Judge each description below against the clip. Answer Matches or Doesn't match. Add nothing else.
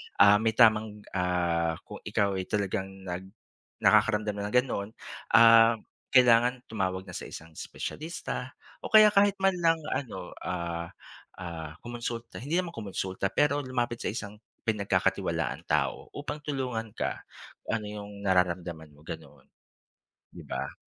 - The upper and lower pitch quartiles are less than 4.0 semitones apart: Doesn't match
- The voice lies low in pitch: Matches